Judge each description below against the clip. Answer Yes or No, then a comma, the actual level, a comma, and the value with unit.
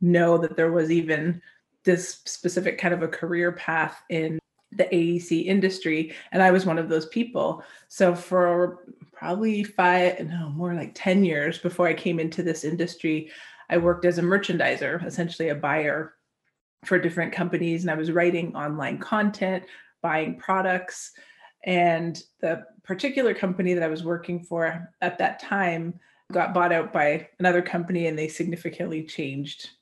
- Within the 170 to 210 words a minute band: No, average, 160 wpm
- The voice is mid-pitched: Yes, medium, 175 Hz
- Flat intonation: Yes, narrow, 1.8 semitones